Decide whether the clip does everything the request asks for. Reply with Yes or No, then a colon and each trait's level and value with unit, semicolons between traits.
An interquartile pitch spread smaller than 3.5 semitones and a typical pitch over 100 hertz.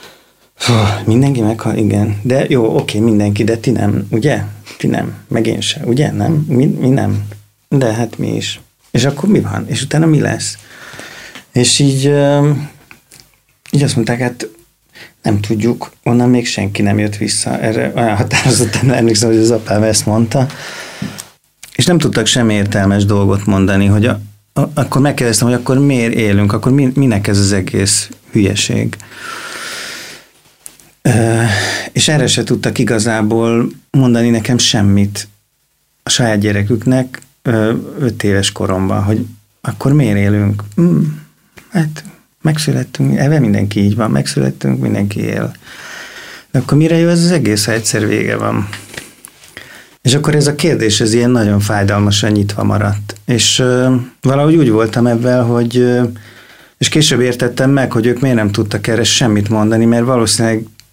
No: average, 3.9 semitones; low, 115 Hz